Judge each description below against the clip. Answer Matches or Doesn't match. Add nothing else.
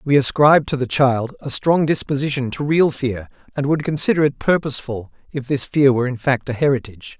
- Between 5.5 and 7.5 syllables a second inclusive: Matches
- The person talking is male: Matches